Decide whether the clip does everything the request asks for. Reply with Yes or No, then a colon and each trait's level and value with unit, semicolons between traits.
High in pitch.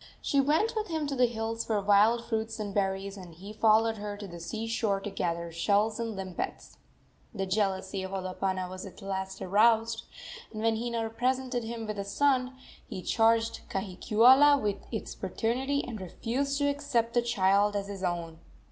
Yes: high, 215 Hz